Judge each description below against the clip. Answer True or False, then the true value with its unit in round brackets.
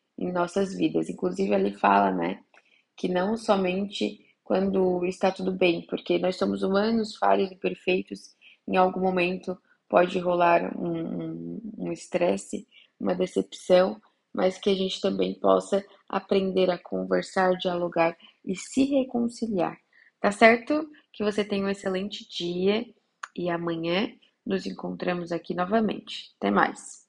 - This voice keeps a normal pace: True (135 wpm)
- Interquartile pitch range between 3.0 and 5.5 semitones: False (2.6 semitones)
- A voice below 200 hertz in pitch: True (185 Hz)